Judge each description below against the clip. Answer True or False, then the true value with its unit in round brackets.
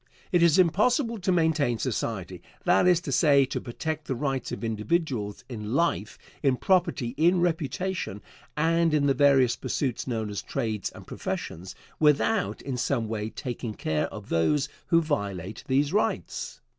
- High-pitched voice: False (140 Hz)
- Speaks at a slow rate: False (155 wpm)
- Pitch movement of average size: False (6.9 semitones)